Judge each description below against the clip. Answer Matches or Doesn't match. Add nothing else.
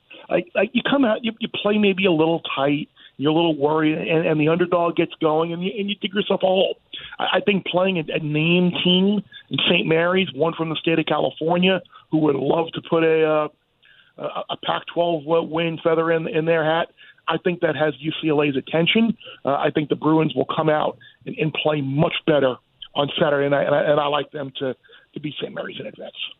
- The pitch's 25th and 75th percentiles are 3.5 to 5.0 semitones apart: Doesn't match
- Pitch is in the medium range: Matches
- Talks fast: Matches